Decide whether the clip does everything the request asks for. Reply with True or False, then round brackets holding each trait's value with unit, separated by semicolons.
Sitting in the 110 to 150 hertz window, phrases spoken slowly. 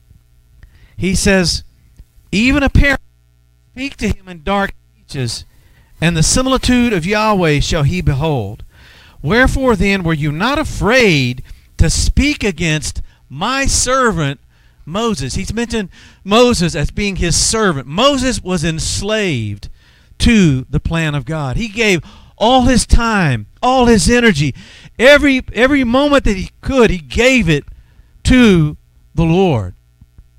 False (175 Hz; 130 wpm)